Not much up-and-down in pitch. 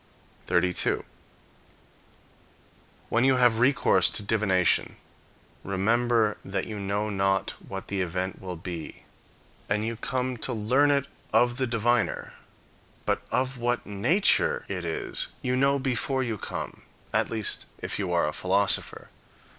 No: average, 4.6 semitones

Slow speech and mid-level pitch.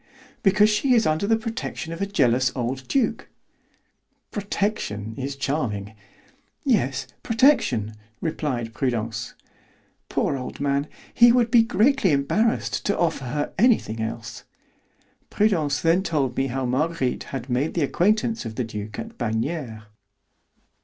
Yes: slow, 130 wpm; medium, 145 Hz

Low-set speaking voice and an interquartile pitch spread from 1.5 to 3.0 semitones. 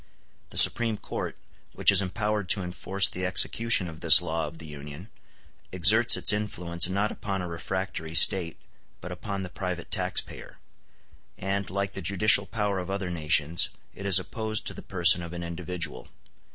Yes: very low, 90 Hz; average, 2.7 semitones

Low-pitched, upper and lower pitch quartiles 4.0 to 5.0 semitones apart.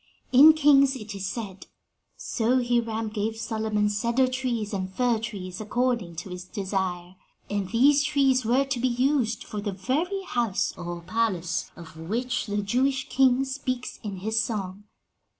No: high, 225 Hz; average, 4.5 semitones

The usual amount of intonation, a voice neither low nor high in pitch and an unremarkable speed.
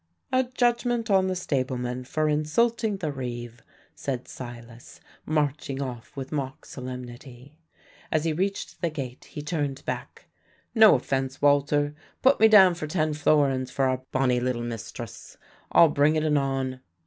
Yes: average, 4.1 semitones; medium, 145 Hz; average, 150 wpm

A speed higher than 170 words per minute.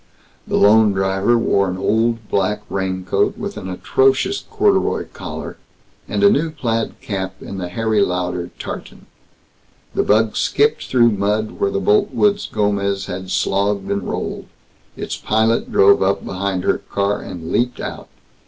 No: average, 150 wpm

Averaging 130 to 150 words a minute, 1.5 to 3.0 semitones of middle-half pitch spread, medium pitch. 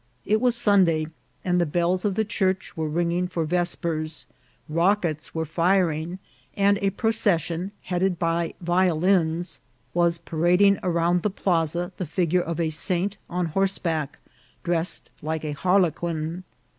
Yes: average, 145 wpm; narrow, 2.4 semitones; medium, 175 Hz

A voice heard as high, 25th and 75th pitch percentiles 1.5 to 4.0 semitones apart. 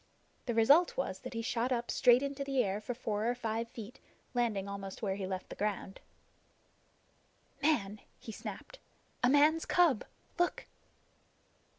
No: high, 235 Hz; average, 4.8 semitones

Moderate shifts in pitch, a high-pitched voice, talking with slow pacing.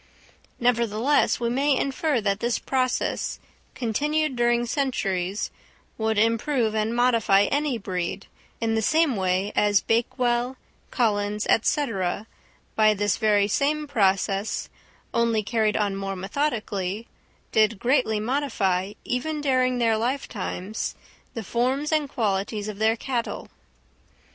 Yes: average, 3.8 semitones; high, 230 Hz; slow, 120 wpm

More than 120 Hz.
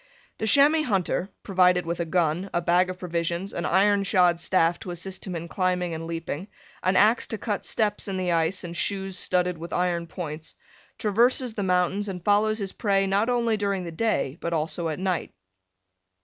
Yes: medium, 185 Hz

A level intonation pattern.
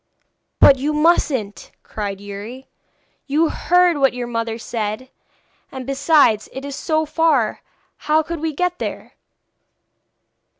No: wide, 5.4 semitones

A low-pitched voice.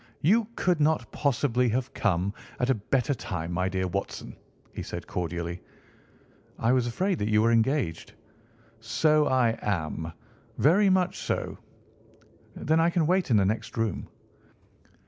Yes: low, 120 Hz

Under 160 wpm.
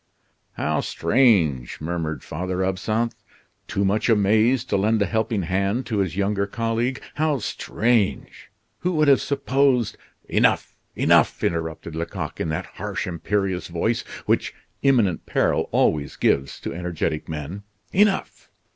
Yes: slow, 135 wpm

